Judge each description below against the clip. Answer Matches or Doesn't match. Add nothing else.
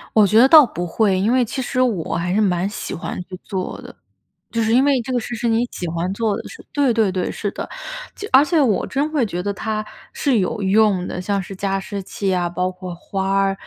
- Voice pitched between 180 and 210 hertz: Matches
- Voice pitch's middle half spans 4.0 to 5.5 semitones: Matches